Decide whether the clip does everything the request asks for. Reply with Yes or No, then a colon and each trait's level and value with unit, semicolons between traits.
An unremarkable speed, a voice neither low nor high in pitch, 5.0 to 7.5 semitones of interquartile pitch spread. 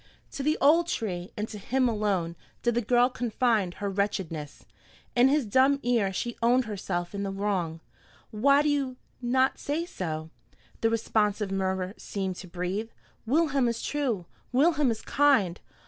No: average, 160 wpm; high, 220 Hz; average, 5.3 semitones